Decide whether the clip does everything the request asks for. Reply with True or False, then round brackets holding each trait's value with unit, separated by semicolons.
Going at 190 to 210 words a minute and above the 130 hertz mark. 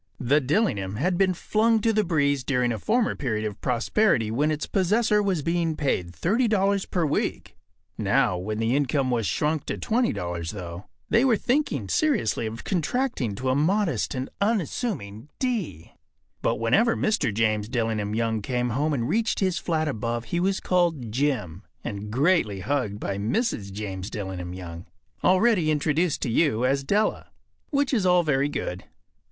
False (165 wpm; 140 Hz)